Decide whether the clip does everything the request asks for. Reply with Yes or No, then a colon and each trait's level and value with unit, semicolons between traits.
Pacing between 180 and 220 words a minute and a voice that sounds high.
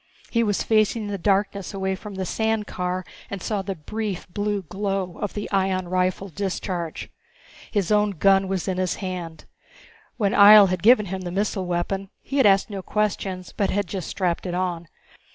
Yes: average, 185 wpm; high, 195 Hz